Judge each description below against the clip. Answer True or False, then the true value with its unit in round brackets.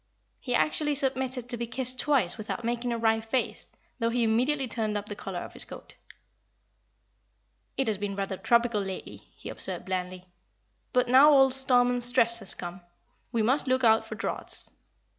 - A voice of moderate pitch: False (235 Hz)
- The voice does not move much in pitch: False (3.2 semitones)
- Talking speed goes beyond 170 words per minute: True (180 wpm)